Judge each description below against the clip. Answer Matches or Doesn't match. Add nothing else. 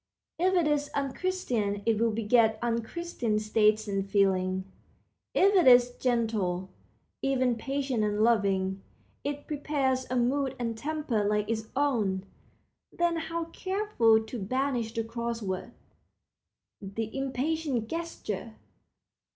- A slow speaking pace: Matches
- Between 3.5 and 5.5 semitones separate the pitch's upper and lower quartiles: Matches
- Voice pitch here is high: Matches